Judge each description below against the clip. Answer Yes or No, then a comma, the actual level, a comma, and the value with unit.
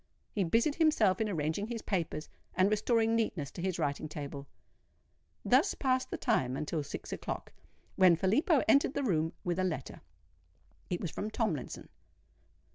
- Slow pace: No, average, 155 wpm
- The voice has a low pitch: No, medium, 185 Hz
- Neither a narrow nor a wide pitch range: No, wide, 6.3 semitones